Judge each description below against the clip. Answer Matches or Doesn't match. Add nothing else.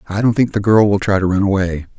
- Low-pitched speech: Matches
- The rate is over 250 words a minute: Matches